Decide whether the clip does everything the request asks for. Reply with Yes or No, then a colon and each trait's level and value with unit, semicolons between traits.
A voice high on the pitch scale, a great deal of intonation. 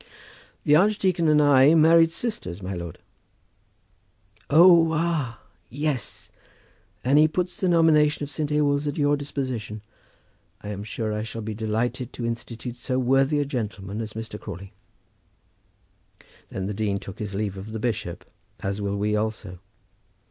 No: low, 125 Hz; wide, 6.1 semitones